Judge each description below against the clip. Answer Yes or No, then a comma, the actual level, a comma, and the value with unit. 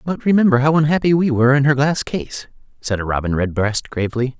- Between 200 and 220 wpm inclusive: Yes, fast, 205 wpm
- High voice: No, low, 135 Hz